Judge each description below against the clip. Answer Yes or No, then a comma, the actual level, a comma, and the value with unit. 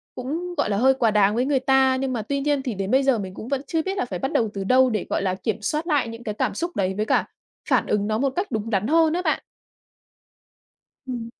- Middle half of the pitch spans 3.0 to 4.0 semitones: No, average, 4.7 semitones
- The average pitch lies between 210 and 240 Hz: No, very high, 255 Hz